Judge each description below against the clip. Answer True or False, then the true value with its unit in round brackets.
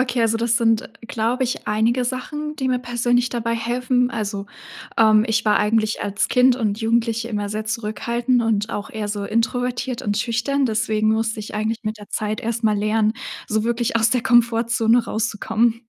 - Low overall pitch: False (225 Hz)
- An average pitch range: False (1.9 semitones)